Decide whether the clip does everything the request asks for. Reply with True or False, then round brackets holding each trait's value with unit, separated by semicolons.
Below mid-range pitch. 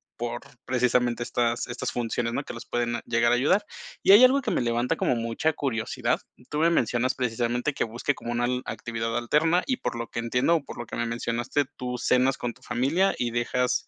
True (120 Hz)